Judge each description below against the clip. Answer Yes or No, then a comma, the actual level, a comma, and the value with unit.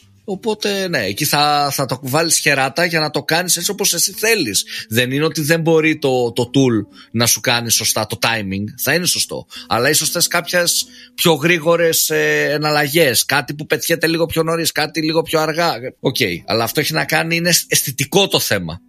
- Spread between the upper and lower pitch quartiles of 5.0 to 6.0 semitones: No, average, 4.1 semitones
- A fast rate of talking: Yes, fast, 190 wpm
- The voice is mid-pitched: Yes, medium, 155 Hz